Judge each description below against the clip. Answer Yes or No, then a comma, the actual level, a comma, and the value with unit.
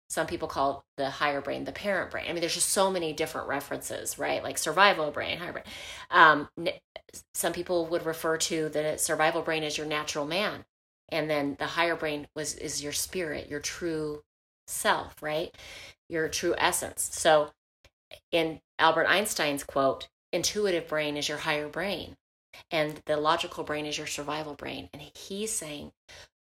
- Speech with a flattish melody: Yes, narrow, 1.9 semitones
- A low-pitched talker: No, medium, 155 Hz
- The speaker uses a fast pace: No, average, 170 wpm